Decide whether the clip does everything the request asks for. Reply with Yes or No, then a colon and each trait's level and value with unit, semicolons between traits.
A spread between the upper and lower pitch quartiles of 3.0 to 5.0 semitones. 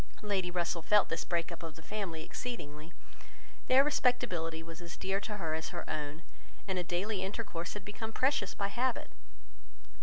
Yes: average, 4.2 semitones